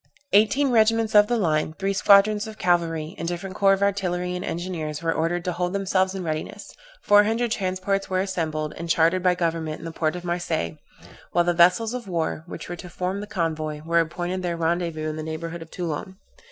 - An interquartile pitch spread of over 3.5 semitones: No, average, 3.1 semitones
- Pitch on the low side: No, medium, 175 Hz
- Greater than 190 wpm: Yes, fast, 205 wpm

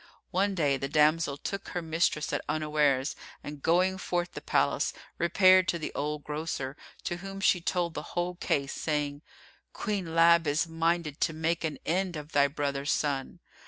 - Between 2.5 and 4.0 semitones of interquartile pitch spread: Yes, average, 3.1 semitones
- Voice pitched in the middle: Yes, medium, 160 Hz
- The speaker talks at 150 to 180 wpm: Yes, average, 170 wpm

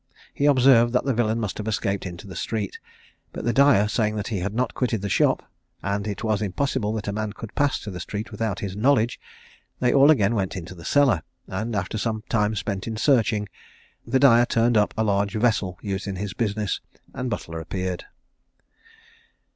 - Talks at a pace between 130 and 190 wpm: No, average, 200 wpm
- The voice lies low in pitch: Yes, low, 110 Hz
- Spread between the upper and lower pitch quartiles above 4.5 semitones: No, average, 3.0 semitones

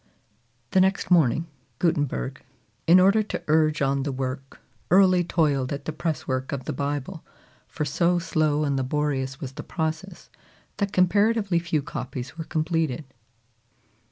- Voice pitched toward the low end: No, medium, 155 Hz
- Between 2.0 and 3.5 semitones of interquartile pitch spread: No, average, 4.1 semitones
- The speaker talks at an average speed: Yes, average, 145 wpm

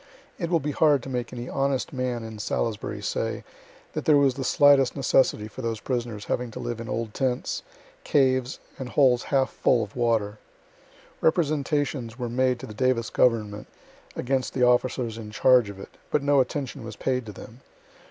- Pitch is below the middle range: Yes, low, 125 Hz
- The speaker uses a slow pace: No, average, 180 wpm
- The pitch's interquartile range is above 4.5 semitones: No, average, 2.8 semitones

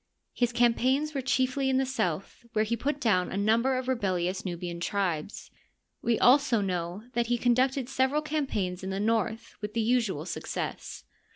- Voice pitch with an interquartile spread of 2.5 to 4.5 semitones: No, average, 5.2 semitones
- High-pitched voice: Yes, high, 230 Hz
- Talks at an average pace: Yes, average, 170 wpm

